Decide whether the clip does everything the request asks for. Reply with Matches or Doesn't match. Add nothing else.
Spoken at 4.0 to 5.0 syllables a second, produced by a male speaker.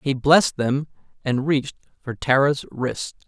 Matches